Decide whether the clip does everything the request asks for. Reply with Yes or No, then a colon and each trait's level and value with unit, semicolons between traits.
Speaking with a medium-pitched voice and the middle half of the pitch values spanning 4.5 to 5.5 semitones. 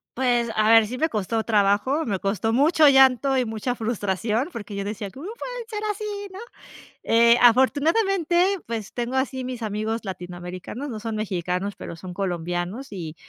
No: high, 230 Hz; average, 4.9 semitones